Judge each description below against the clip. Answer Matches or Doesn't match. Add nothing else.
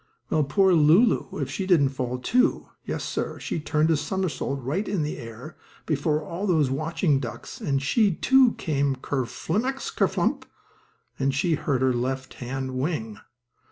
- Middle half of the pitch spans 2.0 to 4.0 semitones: Doesn't match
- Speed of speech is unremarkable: Matches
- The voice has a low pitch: Doesn't match